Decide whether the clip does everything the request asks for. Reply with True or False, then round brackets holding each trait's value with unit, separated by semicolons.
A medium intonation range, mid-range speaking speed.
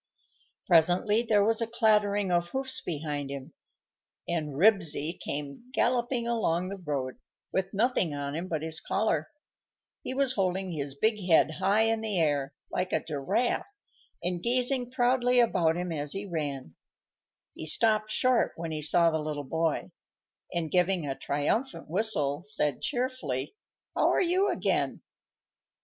False (6.8 semitones; 150 wpm)